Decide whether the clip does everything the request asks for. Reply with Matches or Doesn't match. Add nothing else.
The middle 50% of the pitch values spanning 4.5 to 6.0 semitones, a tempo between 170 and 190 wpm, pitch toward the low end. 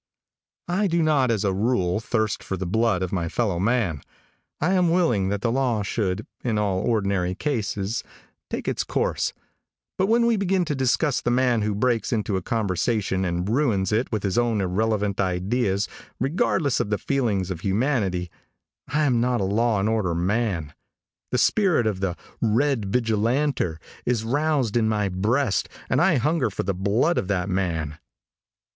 Matches